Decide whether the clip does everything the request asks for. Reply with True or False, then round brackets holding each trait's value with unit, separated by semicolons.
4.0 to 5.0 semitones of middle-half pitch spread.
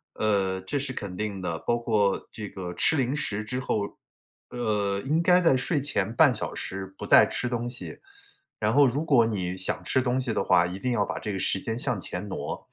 True (4.6 semitones)